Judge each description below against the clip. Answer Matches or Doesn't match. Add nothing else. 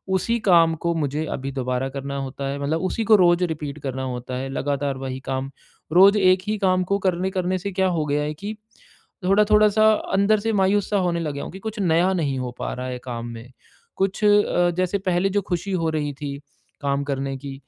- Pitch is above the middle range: Doesn't match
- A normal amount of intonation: Doesn't match